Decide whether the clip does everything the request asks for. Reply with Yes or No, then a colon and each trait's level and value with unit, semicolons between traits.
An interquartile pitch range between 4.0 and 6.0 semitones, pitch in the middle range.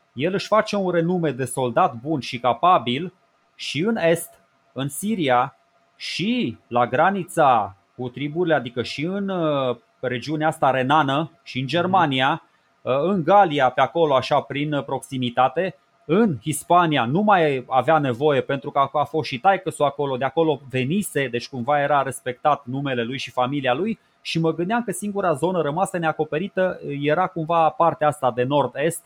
Yes: average, 4.4 semitones; medium, 150 Hz